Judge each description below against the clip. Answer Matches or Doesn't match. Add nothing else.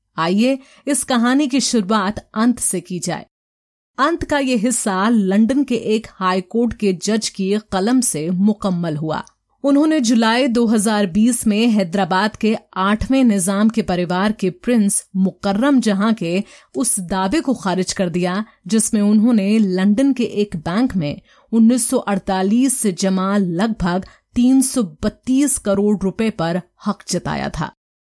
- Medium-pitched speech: Doesn't match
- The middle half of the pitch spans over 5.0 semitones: Doesn't match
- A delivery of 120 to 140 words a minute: Matches